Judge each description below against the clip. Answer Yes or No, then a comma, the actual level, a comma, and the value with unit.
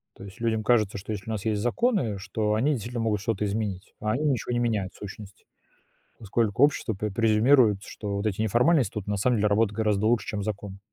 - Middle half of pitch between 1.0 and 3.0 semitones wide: Yes, narrow, 2.5 semitones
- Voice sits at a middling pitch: No, low, 110 Hz